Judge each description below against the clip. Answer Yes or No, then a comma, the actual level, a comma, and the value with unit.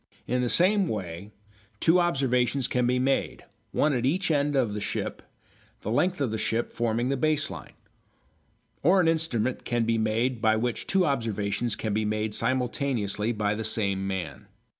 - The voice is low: Yes, low, 120 Hz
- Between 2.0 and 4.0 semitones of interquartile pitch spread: No, average, 4.4 semitones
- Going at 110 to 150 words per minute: No, average, 175 wpm